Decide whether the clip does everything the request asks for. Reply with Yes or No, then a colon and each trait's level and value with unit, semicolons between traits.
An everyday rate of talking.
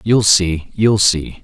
Yes: average, 170 wpm